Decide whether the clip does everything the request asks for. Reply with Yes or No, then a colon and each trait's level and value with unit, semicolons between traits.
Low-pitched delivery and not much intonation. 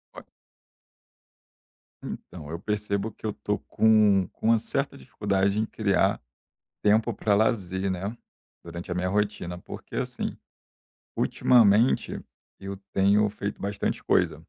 Yes: low, 100 Hz; narrow, 2.1 semitones